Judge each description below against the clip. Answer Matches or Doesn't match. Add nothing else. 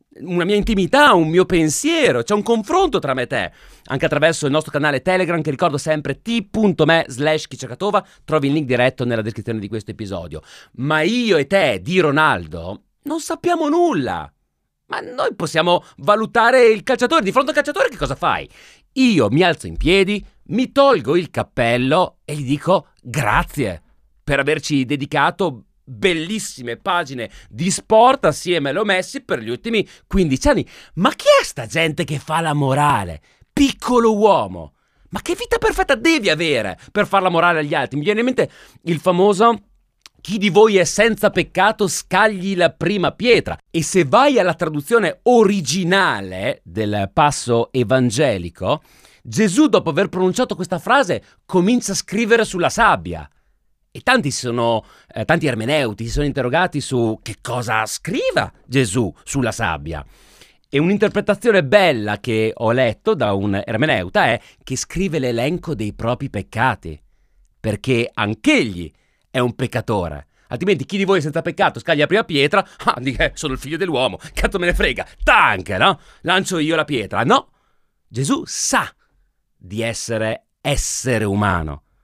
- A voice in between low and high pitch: Matches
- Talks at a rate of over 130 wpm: Matches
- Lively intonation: Matches